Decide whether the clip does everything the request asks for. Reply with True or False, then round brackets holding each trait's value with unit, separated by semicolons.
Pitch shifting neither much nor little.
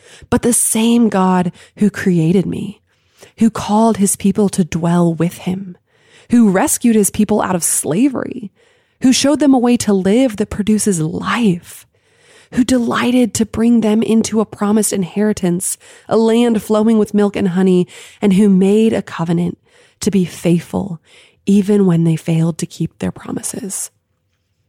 True (3.9 semitones)